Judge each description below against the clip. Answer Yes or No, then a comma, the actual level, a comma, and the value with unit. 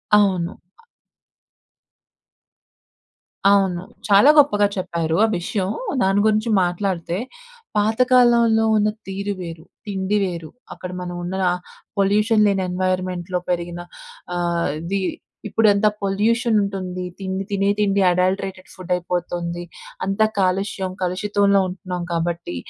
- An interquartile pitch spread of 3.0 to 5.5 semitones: No, narrow, 2.4 semitones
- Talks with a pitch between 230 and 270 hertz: No, high, 190 Hz